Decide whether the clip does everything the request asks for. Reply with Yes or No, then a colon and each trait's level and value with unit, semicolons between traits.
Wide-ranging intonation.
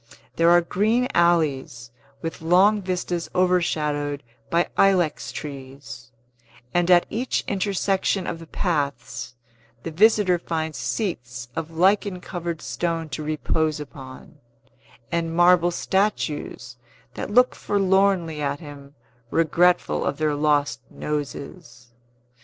No: average, 3.9 semitones